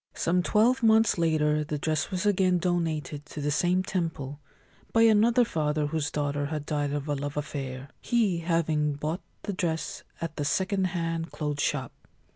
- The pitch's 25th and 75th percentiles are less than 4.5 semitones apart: Yes, average, 3.7 semitones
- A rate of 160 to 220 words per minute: Yes, average, 170 wpm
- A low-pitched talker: No, medium, 160 Hz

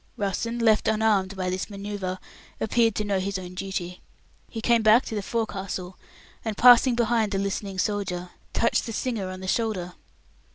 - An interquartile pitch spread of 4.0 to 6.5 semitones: No, average, 3.0 semitones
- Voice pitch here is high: Yes, high, 205 Hz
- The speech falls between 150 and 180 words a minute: Yes, average, 170 wpm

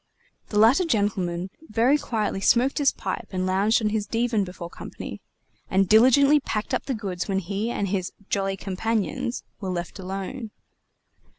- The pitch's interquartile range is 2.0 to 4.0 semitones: Yes, average, 3.4 semitones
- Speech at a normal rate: Yes, average, 160 wpm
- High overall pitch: Yes, high, 210 Hz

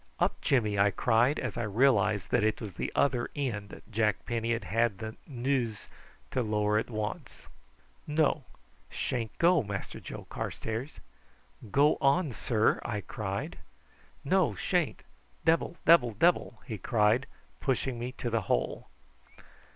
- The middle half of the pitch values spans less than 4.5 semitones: Yes, average, 3.9 semitones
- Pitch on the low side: Yes, low, 115 Hz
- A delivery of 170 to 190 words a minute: No, average, 140 wpm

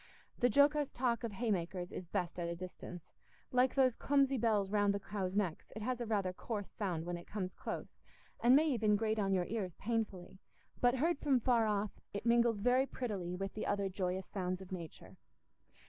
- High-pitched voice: Yes, high, 210 Hz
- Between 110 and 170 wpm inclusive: No, average, 200 wpm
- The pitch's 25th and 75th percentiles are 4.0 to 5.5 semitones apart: Yes, average, 4.5 semitones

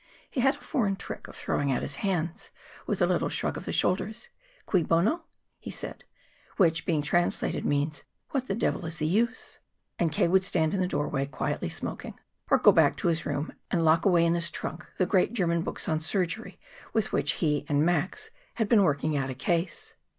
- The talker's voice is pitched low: No, medium, 170 Hz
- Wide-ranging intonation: No, average, 4.0 semitones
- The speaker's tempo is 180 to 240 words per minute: Yes, average, 200 wpm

